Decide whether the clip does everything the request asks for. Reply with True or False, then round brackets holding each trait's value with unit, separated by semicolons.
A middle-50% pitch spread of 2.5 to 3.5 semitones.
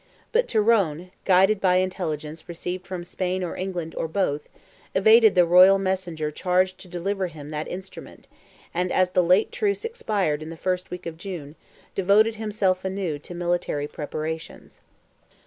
True (2.8 semitones)